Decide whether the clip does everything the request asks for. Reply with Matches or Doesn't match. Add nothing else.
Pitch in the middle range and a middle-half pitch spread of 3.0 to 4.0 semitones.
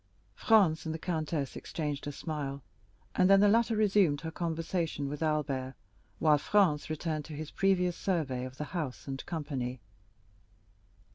Matches